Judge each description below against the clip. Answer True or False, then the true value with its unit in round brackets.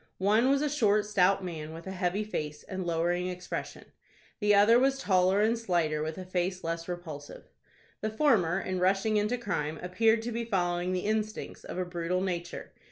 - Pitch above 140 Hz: True (185 Hz)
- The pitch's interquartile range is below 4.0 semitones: True (3.5 semitones)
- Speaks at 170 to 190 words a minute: True (185 wpm)